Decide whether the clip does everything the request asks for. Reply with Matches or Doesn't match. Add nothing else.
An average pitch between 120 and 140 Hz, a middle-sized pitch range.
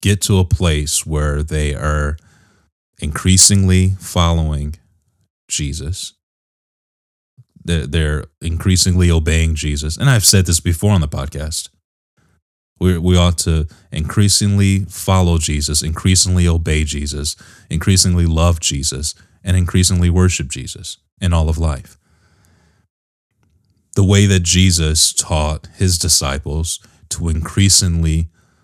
Doesn't match